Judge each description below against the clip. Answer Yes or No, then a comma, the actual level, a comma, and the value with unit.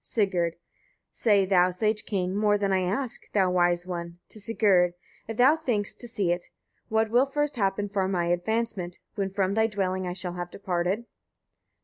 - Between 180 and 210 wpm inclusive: Yes, average, 185 wpm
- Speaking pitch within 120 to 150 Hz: No, high, 195 Hz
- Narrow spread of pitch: No, average, 3.5 semitones